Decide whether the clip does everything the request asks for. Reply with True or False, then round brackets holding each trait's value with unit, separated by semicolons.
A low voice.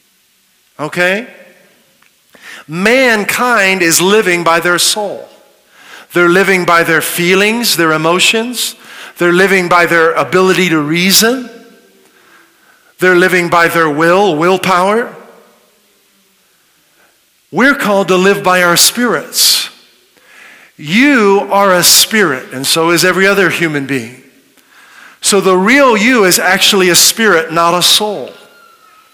False (185 Hz)